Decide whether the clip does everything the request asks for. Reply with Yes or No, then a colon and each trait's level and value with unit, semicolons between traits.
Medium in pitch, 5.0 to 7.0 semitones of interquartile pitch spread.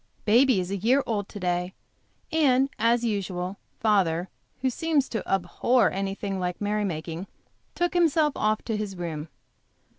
No: high, 205 Hz; wide, 5.4 semitones